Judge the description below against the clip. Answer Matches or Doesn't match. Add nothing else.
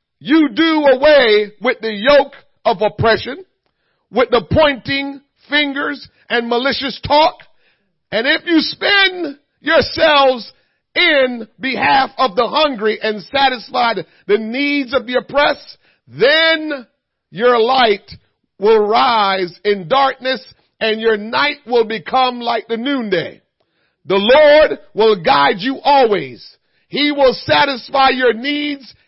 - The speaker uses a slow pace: Matches